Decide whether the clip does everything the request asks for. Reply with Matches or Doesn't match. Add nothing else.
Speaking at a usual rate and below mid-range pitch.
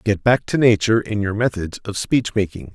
Doesn't match